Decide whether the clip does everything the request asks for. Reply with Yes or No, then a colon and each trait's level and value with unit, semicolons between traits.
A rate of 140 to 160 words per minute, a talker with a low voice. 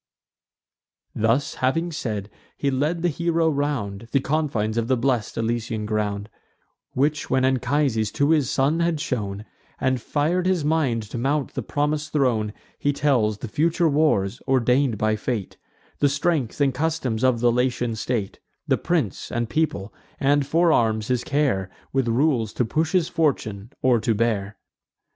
Yes: average, 155 wpm; low, 130 Hz